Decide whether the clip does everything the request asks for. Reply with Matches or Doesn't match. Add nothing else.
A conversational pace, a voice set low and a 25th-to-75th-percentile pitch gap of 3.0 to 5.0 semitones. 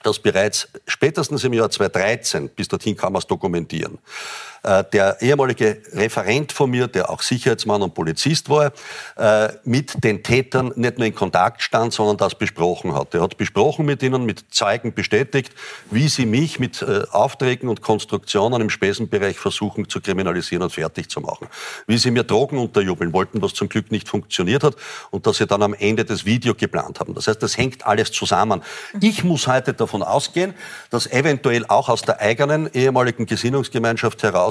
Matches